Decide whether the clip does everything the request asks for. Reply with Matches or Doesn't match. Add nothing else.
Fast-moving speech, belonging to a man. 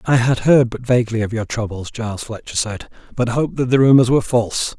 Matches